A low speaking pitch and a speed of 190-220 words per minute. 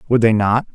No: low, 115 Hz; fast, 245 wpm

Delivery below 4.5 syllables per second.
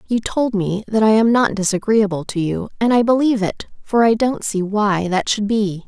No: 4.8 syllables/s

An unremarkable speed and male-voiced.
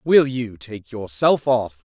Yes: average, 155 wpm; male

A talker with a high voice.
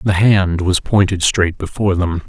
No: very low, 95 Hz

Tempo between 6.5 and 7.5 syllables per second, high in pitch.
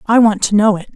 No: 6.1 syllables/s; high, 210 Hz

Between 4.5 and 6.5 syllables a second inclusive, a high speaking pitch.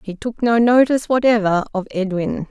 Yes: 5.2 syllables/s; high, 220 Hz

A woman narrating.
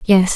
Yes: female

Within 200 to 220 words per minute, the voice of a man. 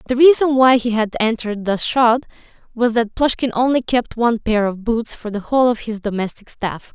No: fast, 205 wpm; female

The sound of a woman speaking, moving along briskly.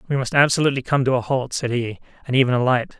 No: male; fast, 240 wpm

